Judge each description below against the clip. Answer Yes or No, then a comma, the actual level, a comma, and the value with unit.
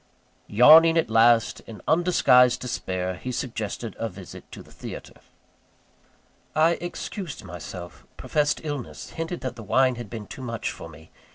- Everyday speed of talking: Yes, average, 150 wpm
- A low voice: Yes, low, 120 Hz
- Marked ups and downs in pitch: Yes, wide, 6.4 semitones